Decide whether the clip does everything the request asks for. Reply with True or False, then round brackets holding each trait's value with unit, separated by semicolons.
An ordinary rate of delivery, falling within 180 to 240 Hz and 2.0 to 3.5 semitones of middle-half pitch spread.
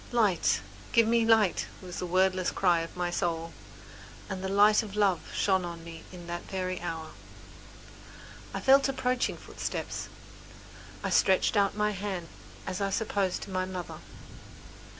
True (150 wpm; 190 Hz; 2.9 semitones)